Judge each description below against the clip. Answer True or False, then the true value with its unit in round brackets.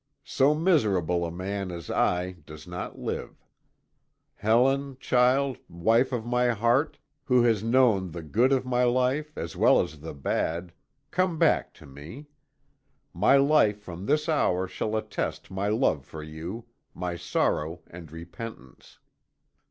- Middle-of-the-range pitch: False (105 Hz)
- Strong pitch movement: True (6.8 semitones)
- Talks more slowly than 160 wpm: True (145 wpm)